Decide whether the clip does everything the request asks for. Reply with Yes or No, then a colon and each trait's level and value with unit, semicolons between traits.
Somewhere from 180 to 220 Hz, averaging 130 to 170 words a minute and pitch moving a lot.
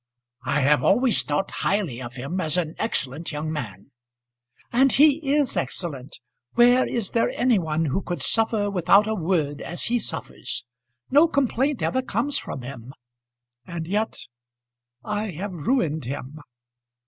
Yes: medium, 185 Hz; average, 150 wpm; wide, 8.2 semitones